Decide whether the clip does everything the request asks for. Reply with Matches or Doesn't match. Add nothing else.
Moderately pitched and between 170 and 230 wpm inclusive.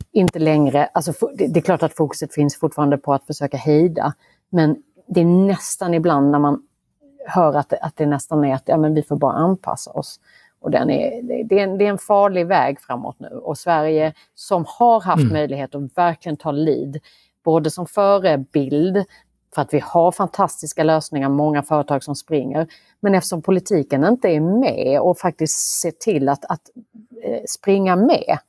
Matches